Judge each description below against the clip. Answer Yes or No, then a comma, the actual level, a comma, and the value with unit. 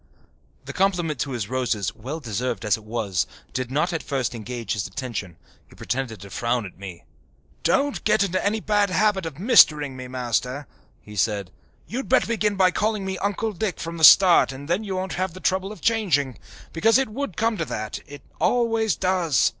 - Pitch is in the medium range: Yes, medium, 160 Hz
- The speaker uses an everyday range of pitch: No, wide, 8.7 semitones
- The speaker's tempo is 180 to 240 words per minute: Yes, average, 195 wpm